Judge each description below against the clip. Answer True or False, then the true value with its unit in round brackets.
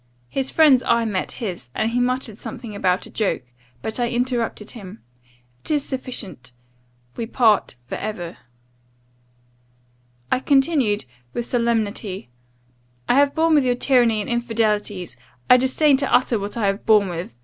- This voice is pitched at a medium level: False (230 Hz)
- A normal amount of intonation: True (3.7 semitones)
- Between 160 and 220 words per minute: False (150 wpm)